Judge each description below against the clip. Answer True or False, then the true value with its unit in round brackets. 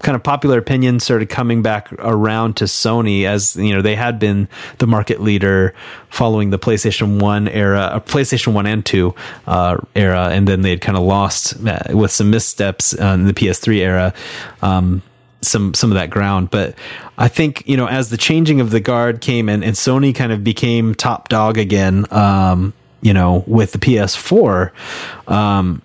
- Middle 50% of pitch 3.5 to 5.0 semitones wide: False (3.1 semitones)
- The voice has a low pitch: True (105 Hz)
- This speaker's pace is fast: False (190 wpm)